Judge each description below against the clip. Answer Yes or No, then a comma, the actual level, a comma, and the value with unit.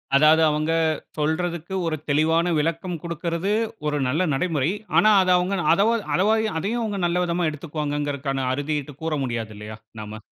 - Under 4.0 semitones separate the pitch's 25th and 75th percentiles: Yes, average, 3.5 semitones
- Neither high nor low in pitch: Yes, medium, 160 Hz